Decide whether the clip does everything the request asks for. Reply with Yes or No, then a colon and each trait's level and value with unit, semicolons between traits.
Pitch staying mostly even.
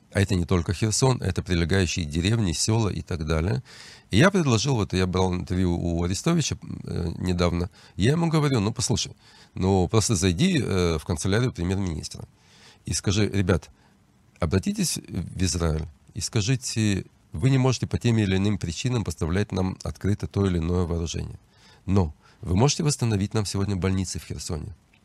No: average, 3.9 semitones